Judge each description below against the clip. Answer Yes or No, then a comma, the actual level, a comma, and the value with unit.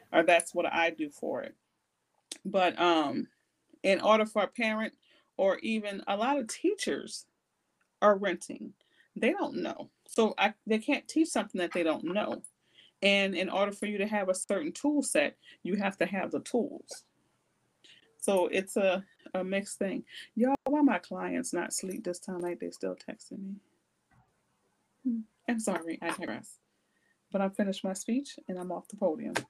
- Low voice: No, high, 200 Hz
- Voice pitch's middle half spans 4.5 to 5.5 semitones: Yes, average, 5.1 semitones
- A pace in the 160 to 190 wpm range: Yes, average, 175 wpm